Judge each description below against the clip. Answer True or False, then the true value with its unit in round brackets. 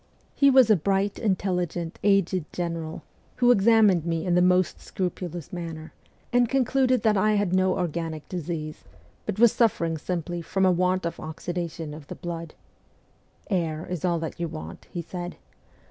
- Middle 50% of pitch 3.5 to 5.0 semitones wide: False (3.0 semitones)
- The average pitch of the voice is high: False (180 Hz)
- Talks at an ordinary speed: True (170 wpm)